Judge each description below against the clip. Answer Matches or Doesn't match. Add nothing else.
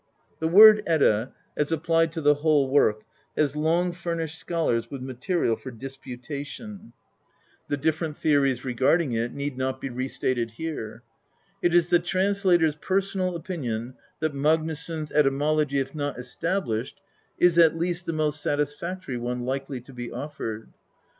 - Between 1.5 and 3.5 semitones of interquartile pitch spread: Doesn't match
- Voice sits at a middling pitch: Matches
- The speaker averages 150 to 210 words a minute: Matches